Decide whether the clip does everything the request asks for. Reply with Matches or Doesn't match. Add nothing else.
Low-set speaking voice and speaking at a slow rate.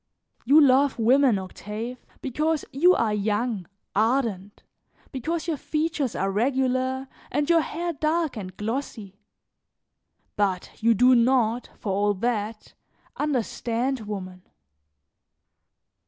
Doesn't match